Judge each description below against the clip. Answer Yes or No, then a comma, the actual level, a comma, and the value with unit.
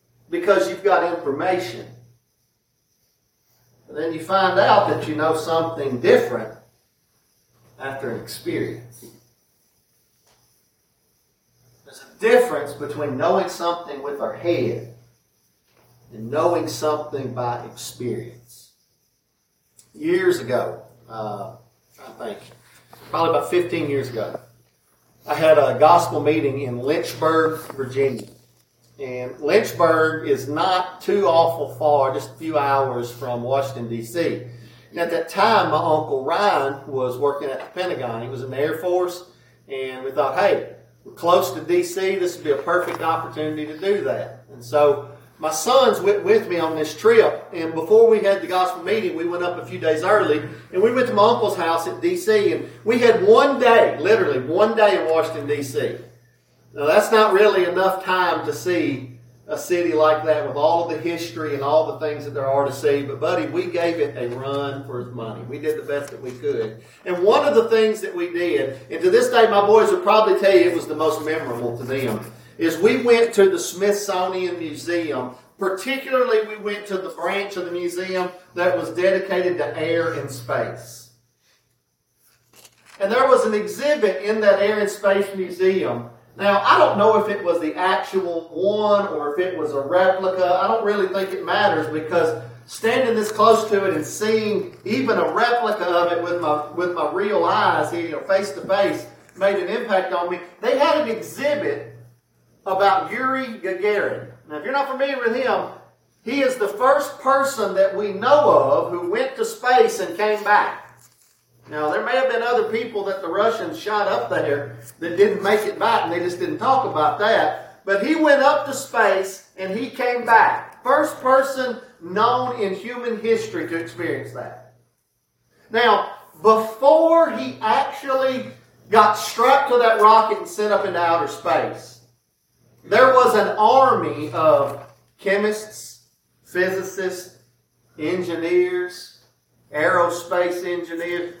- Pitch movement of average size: No, wide, 6.2 semitones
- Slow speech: No, average, 165 wpm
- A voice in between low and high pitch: Yes, medium, 180 Hz